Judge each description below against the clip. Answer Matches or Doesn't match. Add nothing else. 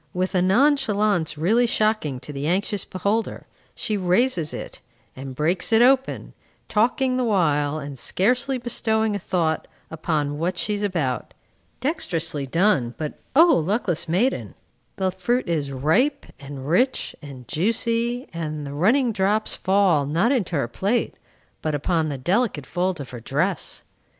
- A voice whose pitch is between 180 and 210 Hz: Matches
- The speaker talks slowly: Doesn't match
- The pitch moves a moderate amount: Doesn't match